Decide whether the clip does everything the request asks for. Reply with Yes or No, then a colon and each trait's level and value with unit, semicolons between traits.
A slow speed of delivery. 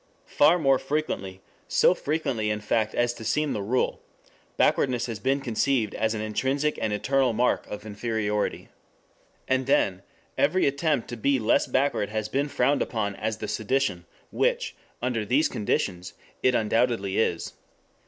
No: average, 155 wpm